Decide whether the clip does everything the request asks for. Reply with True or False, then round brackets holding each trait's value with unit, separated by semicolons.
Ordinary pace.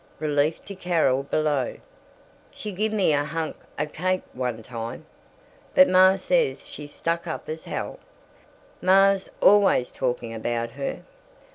False (130 wpm)